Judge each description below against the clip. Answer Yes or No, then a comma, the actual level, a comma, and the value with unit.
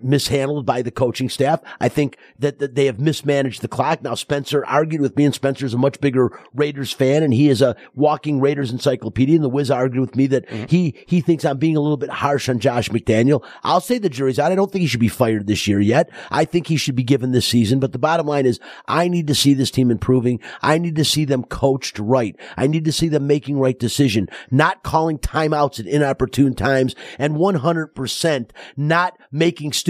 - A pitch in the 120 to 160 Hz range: Yes, medium, 140 Hz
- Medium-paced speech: No, fast, 225 wpm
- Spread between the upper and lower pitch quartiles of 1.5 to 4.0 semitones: Yes, average, 2.8 semitones